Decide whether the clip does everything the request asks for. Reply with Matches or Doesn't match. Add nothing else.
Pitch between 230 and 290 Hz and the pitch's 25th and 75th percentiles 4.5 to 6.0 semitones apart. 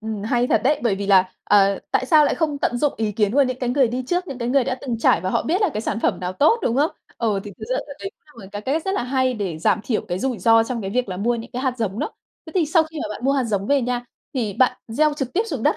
Matches